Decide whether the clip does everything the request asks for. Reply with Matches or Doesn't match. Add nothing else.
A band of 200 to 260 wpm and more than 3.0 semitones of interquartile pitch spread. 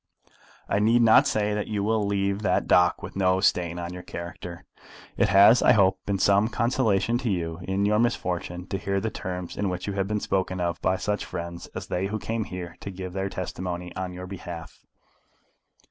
Doesn't match